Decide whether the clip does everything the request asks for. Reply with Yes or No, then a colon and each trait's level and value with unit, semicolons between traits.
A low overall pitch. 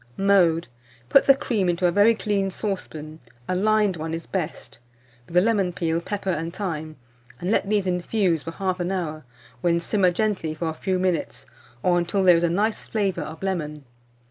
No: medium, 180 Hz